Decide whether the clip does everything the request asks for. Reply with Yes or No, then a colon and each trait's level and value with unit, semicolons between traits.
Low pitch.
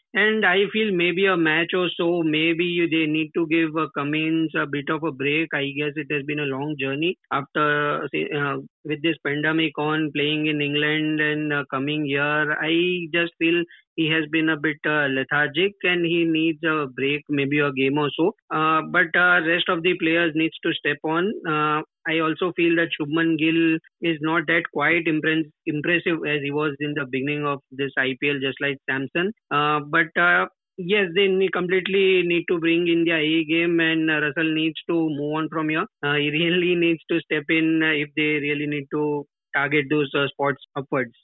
No: medium, 155 Hz